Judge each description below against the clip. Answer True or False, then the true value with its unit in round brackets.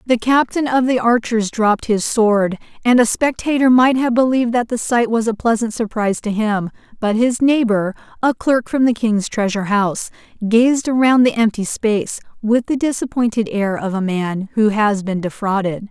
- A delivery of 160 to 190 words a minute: True (185 wpm)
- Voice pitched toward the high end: True (225 Hz)